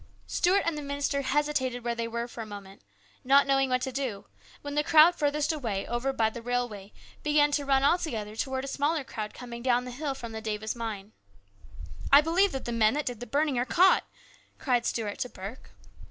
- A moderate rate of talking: No, fast, 215 wpm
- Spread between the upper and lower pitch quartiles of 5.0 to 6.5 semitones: No, average, 3.9 semitones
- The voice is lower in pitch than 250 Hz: No, very high, 255 Hz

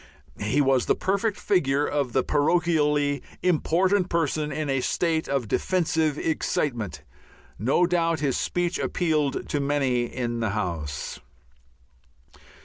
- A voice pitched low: No, medium, 145 Hz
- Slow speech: Yes, slow, 125 wpm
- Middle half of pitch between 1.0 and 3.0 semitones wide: No, average, 4.3 semitones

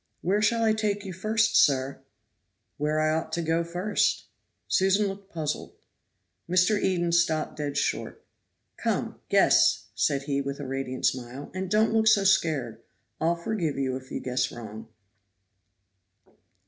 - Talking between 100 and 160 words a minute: Yes, average, 150 wpm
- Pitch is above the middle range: No, medium, 165 Hz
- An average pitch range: No, wide, 6.3 semitones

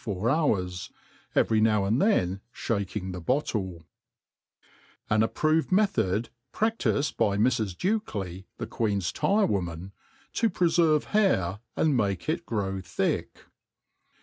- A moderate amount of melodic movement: No, wide, 8.7 semitones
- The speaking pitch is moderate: No, low, 110 Hz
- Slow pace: Yes, slow, 120 wpm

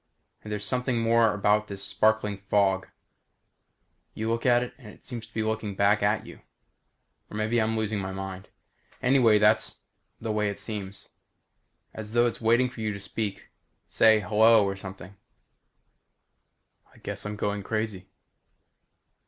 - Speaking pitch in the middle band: No, low, 105 Hz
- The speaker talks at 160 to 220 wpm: Yes, average, 165 wpm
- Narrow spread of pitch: Yes, narrow, 2.0 semitones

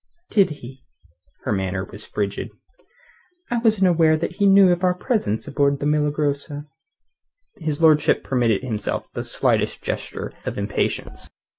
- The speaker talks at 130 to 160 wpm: Yes, average, 140 wpm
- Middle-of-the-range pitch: Yes, medium, 150 Hz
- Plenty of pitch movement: Yes, wide, 6.5 semitones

